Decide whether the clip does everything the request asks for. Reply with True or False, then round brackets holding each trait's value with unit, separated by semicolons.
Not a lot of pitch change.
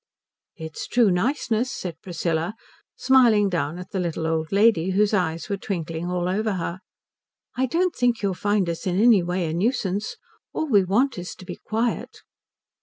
False (4.3 semitones)